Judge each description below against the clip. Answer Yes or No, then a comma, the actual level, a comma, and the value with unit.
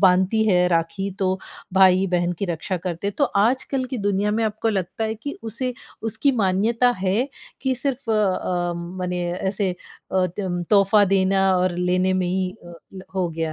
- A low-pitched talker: No, high, 190 Hz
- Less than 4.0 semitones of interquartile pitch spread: Yes, average, 3.2 semitones